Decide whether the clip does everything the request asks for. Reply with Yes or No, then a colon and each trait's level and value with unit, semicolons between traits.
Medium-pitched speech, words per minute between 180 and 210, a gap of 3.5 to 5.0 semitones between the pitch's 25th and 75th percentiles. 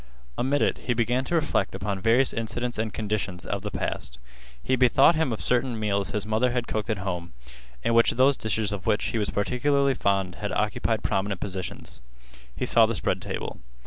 No: low, 110 Hz; average, 195 wpm; average, 3.9 semitones